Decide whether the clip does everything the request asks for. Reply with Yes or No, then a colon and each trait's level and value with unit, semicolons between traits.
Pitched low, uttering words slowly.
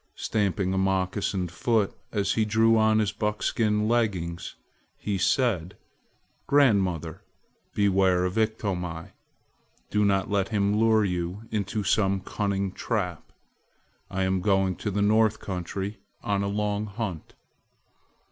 Yes: low, 100 Hz; slow, 125 wpm